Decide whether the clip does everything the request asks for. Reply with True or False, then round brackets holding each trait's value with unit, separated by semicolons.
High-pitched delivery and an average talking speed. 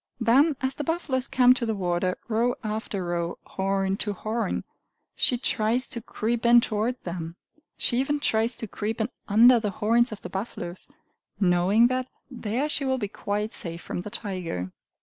True (220 Hz; 175 wpm)